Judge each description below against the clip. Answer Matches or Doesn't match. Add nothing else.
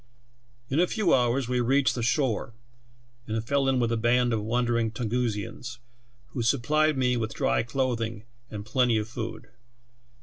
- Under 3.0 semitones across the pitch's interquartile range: Matches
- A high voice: Doesn't match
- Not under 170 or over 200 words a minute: Doesn't match